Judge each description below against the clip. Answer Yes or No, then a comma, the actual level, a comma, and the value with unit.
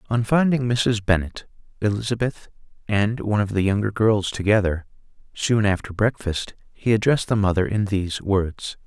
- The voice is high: No, low, 105 Hz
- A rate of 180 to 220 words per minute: No, average, 150 wpm